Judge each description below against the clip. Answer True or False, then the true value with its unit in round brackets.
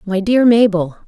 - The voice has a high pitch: True (205 Hz)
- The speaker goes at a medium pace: True (165 wpm)